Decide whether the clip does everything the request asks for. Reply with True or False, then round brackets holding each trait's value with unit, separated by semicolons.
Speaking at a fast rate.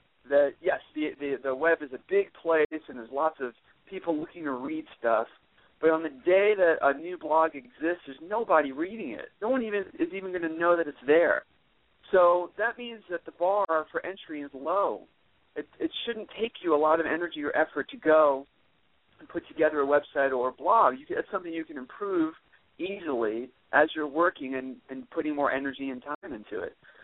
True (210 wpm)